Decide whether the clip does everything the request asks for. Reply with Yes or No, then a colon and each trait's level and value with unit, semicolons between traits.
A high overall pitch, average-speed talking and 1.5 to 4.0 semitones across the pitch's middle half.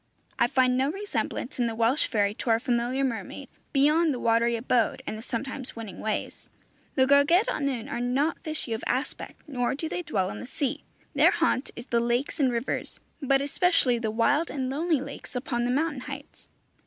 Yes: very high, 260 Hz; average, 190 wpm; average, 3.2 semitones